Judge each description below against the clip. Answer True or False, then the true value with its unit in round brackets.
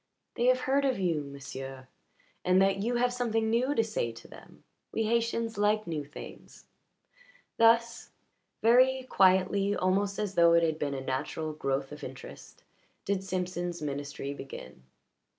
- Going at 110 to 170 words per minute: True (150 wpm)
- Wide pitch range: True (7.5 semitones)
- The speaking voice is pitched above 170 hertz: True (190 Hz)